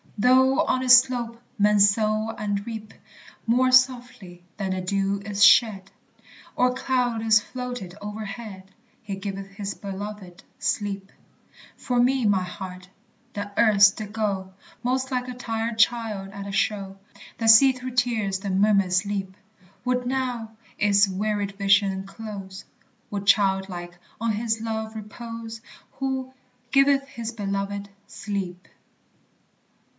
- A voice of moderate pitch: No, high, 210 Hz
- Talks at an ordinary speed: No, slow, 130 wpm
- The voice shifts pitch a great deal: No, average, 3.3 semitones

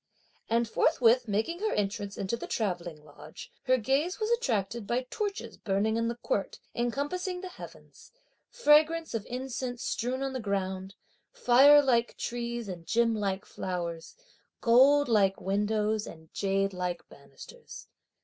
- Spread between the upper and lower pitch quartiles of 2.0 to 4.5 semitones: No, average, 5.3 semitones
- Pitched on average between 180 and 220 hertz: No, high, 230 Hz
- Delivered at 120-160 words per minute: Yes, average, 140 wpm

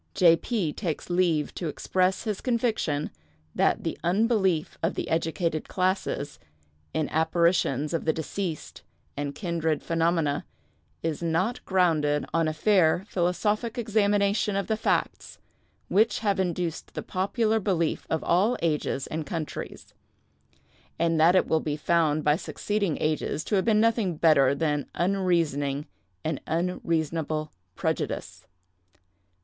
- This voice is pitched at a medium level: Yes, medium, 170 Hz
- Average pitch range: Yes, average, 3.9 semitones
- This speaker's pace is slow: Yes, slow, 130 wpm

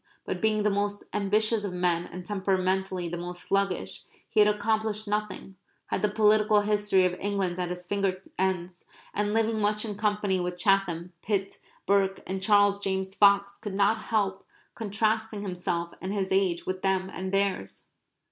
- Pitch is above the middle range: Yes, high, 195 Hz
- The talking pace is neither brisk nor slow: Yes, average, 165 wpm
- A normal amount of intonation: No, narrow, 2.0 semitones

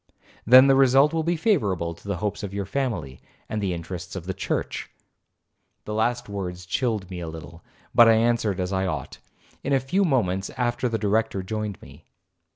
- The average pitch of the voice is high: No, low, 105 Hz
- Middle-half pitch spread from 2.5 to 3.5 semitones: No, average, 5.1 semitones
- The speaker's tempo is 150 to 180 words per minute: No, average, 190 wpm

